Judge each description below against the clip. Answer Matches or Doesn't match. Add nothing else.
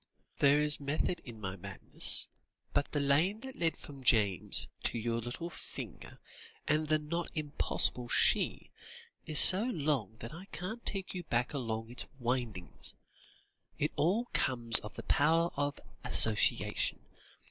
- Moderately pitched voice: Matches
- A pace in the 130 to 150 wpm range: Matches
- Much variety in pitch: Matches